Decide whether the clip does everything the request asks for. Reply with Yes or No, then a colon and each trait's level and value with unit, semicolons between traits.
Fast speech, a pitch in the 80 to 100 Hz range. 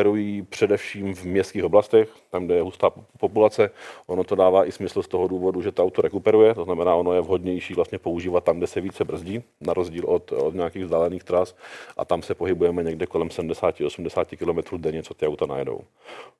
No: fast, 200 wpm; low, 110 Hz